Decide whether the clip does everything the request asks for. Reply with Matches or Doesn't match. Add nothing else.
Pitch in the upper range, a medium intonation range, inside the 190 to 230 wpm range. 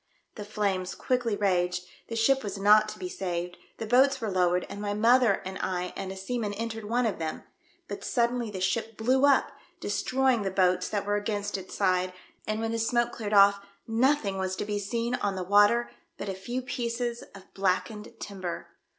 Matches